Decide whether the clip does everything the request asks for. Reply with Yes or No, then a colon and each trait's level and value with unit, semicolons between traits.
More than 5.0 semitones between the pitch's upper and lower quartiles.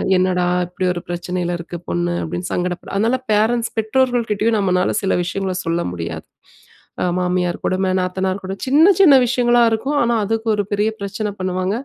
No: average, 3.9 semitones